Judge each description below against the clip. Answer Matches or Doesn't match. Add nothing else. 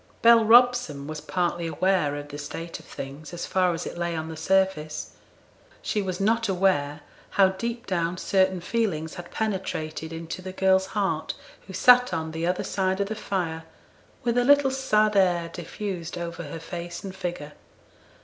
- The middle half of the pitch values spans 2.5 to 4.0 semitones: Matches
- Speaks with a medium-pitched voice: Matches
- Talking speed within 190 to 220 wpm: Doesn't match